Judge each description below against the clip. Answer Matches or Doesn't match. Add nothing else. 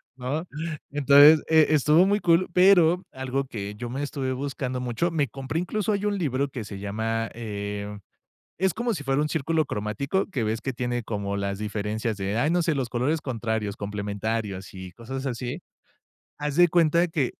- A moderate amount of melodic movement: Doesn't match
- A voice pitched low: Matches